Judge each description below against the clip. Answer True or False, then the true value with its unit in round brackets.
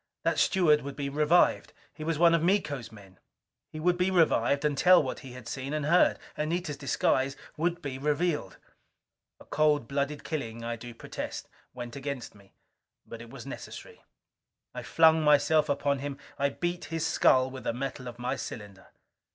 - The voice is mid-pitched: True (145 Hz)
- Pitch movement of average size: True (3.7 semitones)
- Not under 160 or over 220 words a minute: True (175 wpm)